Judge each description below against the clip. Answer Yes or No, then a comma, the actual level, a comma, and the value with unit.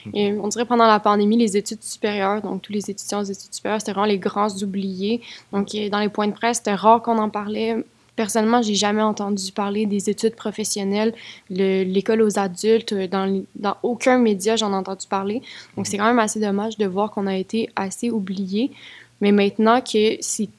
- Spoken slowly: No, average, 200 wpm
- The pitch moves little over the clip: Yes, narrow, 1.8 semitones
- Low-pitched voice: No, high, 210 Hz